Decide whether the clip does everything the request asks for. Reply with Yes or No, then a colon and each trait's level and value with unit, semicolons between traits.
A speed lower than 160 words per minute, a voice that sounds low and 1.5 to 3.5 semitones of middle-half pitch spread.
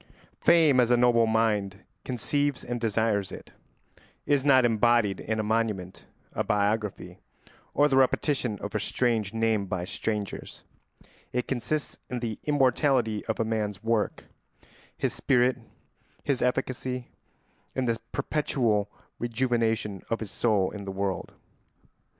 Yes: slow, 135 wpm; low, 115 Hz; average, 3.2 semitones